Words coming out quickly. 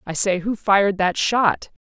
No: average, 195 wpm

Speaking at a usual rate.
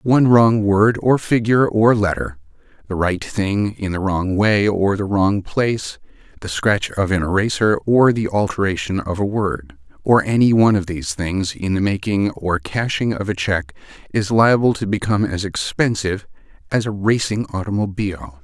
Yes: average, 165 wpm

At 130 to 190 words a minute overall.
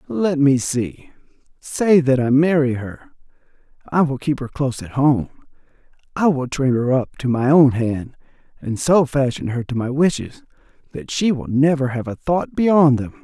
Yes: average, 180 wpm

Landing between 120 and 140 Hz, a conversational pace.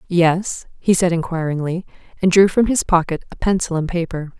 No: medium, 175 Hz; average, 180 wpm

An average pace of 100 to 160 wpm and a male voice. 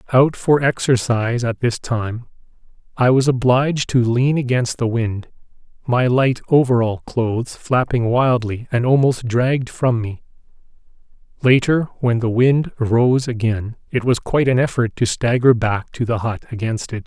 Yes: average, 155 wpm; male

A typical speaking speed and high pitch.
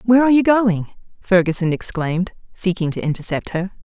Yes: average, 155 wpm; high, 195 Hz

